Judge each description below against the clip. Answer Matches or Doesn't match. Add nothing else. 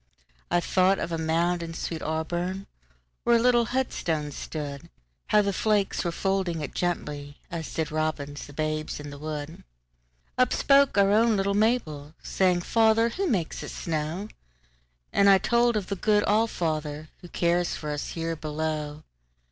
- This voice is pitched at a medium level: Matches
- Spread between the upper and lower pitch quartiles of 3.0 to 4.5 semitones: Doesn't match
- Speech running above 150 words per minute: Doesn't match